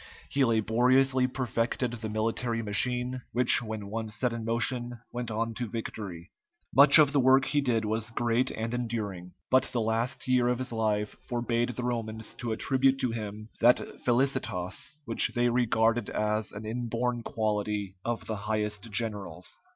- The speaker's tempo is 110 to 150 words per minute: No, average, 160 wpm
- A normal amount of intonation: No, narrow, 2.3 semitones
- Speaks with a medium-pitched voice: No, low, 115 Hz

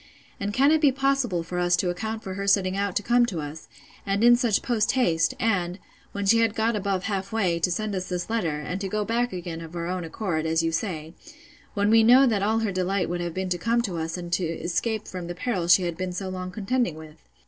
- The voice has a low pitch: No, high, 190 Hz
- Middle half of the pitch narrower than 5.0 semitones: Yes, average, 4.2 semitones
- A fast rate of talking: Yes, fast, 255 wpm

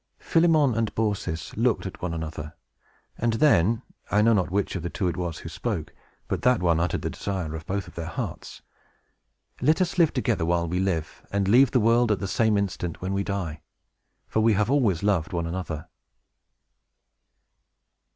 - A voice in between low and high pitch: No, low, 100 Hz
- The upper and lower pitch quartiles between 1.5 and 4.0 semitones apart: No, average, 5.0 semitones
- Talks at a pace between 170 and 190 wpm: Yes, average, 180 wpm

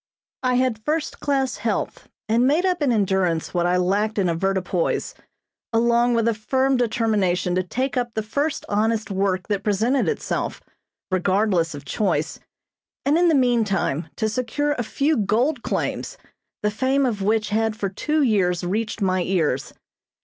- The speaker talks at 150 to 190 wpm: Yes, average, 160 wpm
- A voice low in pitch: No, high, 220 Hz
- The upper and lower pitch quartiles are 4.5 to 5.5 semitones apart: Yes, average, 4.9 semitones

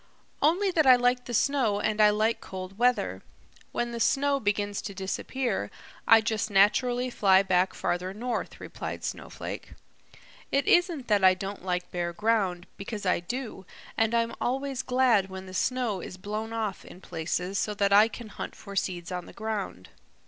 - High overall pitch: Yes, high, 210 Hz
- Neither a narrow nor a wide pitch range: Yes, average, 4.4 semitones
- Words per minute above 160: Yes, average, 175 wpm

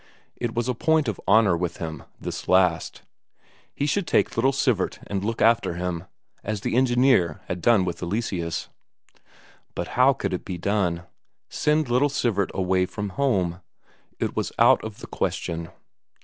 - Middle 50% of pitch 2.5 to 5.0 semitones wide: No, wide, 5.4 semitones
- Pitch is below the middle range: Yes, low, 100 Hz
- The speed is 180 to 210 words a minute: No, average, 165 wpm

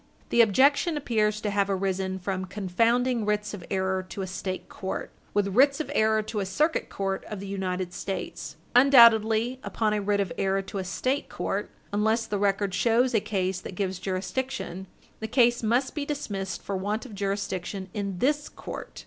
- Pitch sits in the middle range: No, high, 205 Hz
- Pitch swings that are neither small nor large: Yes, average, 3.4 semitones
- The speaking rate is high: No, average, 185 wpm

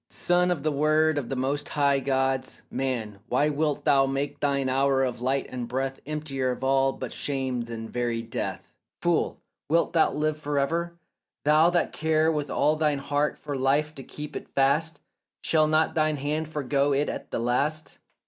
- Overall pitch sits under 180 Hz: Yes, medium, 140 Hz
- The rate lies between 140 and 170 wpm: No, average, 185 wpm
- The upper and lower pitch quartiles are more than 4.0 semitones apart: No, narrow, 2.5 semitones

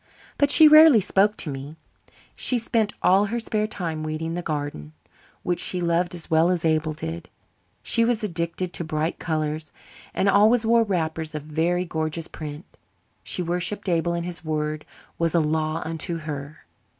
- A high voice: No, medium, 170 Hz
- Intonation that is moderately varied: Yes, average, 3.7 semitones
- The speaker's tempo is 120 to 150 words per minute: No, average, 170 wpm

